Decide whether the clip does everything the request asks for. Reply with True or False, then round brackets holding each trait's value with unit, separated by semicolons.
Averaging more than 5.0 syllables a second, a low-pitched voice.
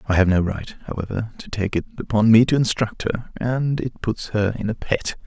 True (5.5 syllables/s; 110 Hz)